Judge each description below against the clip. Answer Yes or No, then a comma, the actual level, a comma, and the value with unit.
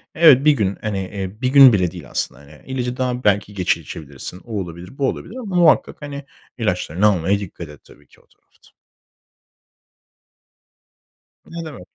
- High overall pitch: No, low, 105 Hz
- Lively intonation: Yes, wide, 6.8 semitones